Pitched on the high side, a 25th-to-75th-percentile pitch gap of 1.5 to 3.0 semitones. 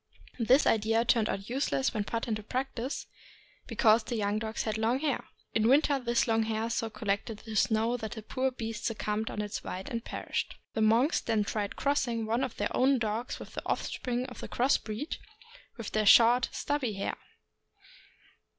Yes: high, 225 Hz; narrow, 2.4 semitones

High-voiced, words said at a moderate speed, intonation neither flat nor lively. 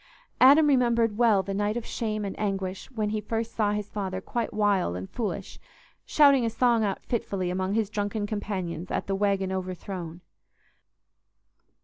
Yes: high, 205 Hz; average, 160 wpm; average, 3.0 semitones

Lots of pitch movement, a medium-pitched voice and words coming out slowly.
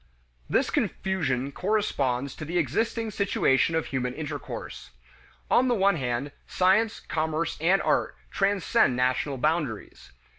Yes: wide, 6.6 semitones; medium, 160 Hz; slow, 120 wpm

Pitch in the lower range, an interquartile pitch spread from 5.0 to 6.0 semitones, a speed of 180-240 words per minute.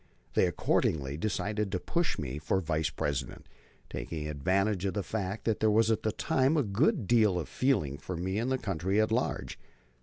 Yes: low, 100 Hz; wide, 5.6 semitones; average, 190 wpm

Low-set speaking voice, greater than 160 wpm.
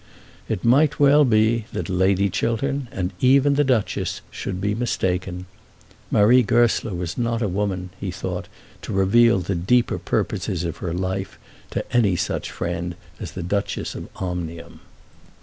No: low, 100 Hz; average, 150 wpm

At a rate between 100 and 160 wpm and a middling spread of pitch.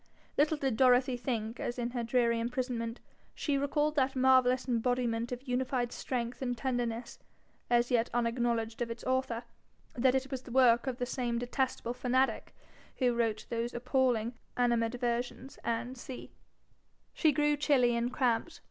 No: average, 150 wpm; narrow, 1.7 semitones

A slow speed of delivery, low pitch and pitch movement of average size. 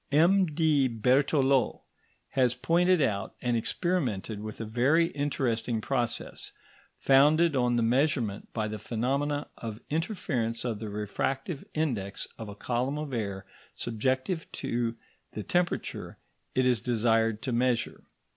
Yes: slow, 125 wpm; low, 125 Hz; average, 4.4 semitones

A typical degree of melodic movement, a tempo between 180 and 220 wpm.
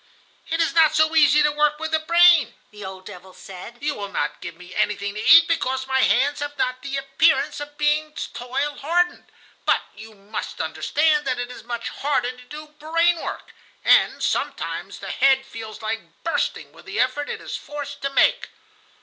Yes: average, 4.2 semitones; average, 190 wpm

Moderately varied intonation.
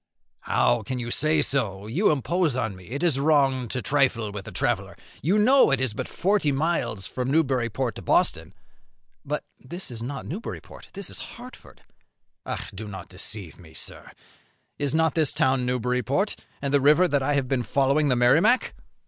Yes: average, 4.4 semitones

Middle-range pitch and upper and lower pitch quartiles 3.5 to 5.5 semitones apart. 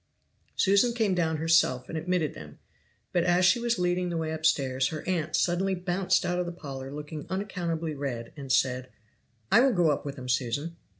Yes: medium, 165 Hz; average, 4.3 semitones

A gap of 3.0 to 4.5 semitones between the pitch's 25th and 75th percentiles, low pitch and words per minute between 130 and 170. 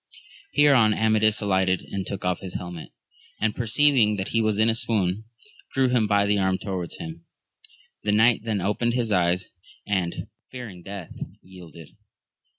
Yes: average, 3.3 semitones; low, 105 Hz; average, 155 wpm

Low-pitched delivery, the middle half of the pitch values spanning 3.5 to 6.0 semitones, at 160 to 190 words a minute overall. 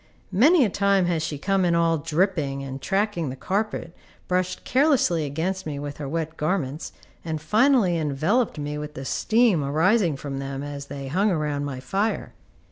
No: medium, 165 Hz; average, 5.3 semitones; average, 175 wpm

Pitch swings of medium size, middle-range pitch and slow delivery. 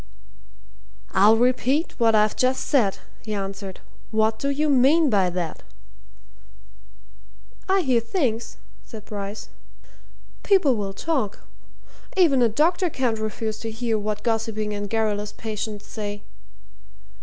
No: average, 3.7 semitones; high, 225 Hz; slow, 120 wpm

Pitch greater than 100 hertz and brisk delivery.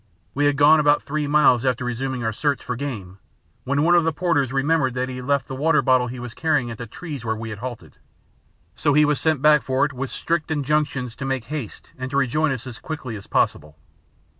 Yes: low, 135 Hz; fast, 235 wpm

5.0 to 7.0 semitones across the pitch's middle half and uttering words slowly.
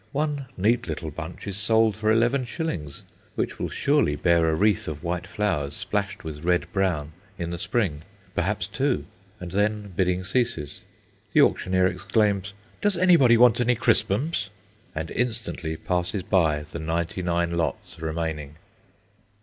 No: average, 5.3 semitones; average, 145 wpm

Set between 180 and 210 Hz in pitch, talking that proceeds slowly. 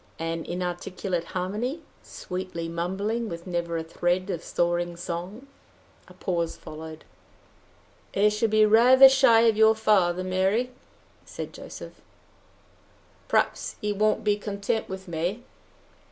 Yes: high, 190 Hz; slow, 125 wpm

